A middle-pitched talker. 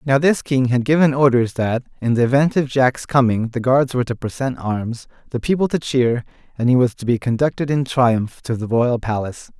No: low, 125 Hz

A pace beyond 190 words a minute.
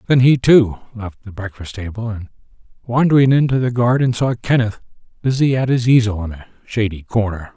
No: average, 175 wpm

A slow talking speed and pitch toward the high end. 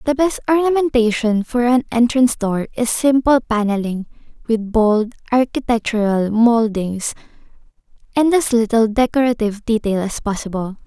Yes: slow, 115 wpm; high, 230 Hz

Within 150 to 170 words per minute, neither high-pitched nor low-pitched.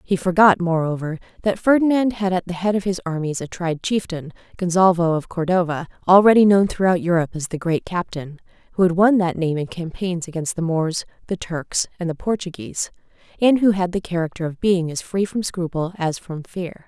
No: average, 195 wpm; medium, 180 Hz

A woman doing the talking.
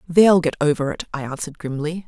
Yes: female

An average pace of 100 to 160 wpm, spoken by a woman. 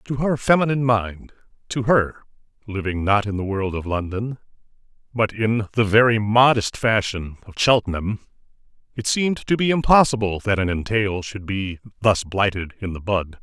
No: average, 150 wpm; male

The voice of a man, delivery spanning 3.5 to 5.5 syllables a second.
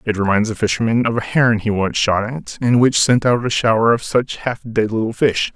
Yes: male; 5.4 syllables/s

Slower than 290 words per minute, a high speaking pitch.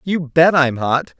No: average, 200 wpm; medium, 150 Hz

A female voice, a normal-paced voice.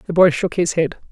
No: female; fast, 270 wpm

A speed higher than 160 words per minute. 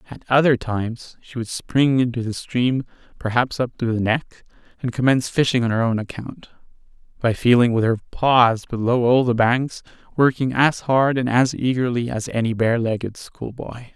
Yes: average, 180 wpm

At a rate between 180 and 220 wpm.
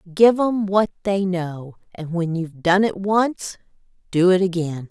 No: average, 170 wpm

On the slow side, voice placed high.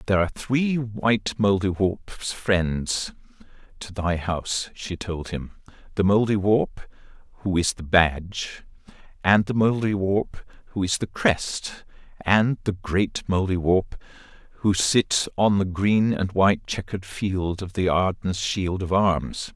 No: slow, 130 wpm; very low, 95 Hz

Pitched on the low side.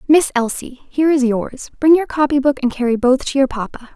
No: very high, 265 Hz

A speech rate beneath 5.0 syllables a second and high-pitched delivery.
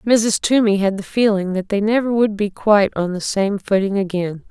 No: 5.1 syllables/s; high, 205 Hz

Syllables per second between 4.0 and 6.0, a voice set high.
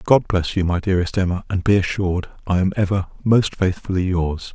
No: 5.7 syllables/s; very low, 95 Hz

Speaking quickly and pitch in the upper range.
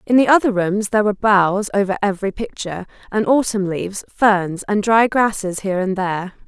No: average, 185 wpm; high, 205 Hz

